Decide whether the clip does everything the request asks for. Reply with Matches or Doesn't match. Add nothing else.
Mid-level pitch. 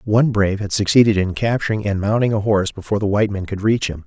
Doesn't match